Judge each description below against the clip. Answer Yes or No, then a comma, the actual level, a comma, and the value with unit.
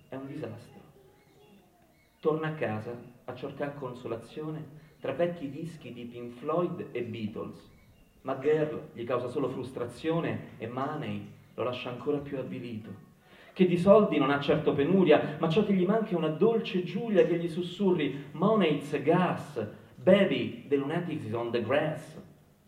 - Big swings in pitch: Yes, wide, 5.7 semitones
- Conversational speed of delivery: Yes, average, 150 wpm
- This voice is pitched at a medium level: Yes, medium, 150 Hz